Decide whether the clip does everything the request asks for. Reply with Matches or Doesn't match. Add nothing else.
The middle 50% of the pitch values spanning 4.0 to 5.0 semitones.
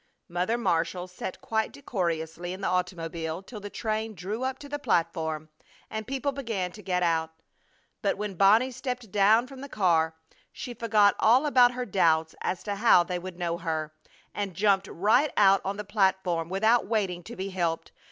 Matches